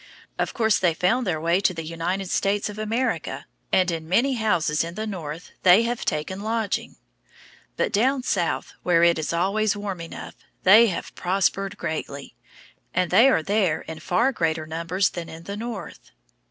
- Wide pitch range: No, average, 4.5 semitones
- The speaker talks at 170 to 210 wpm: Yes, average, 175 wpm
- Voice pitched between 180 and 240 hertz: Yes, medium, 185 Hz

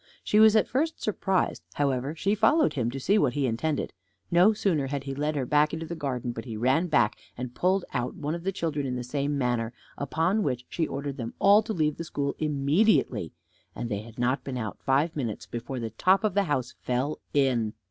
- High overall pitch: No, medium, 140 Hz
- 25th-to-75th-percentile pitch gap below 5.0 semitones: No, wide, 5.4 semitones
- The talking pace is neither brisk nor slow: No, fast, 220 wpm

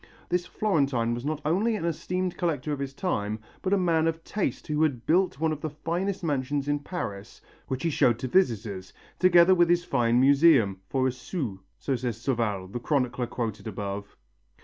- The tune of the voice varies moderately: No, wide, 6.2 semitones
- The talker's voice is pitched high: No, medium, 140 Hz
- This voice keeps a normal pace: Yes, average, 190 wpm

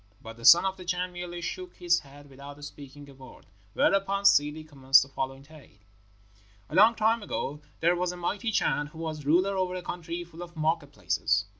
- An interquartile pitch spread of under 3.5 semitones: No, average, 4.1 semitones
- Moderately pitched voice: Yes, medium, 165 Hz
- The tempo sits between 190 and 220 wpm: Yes, average, 200 wpm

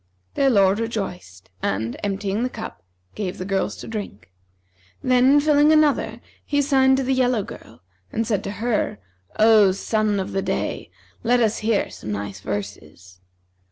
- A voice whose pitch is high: Yes, high, 210 Hz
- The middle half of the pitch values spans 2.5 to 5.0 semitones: No, wide, 5.5 semitones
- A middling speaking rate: Yes, average, 160 wpm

